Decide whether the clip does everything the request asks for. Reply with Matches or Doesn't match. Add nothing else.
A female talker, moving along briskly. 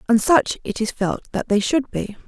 Matches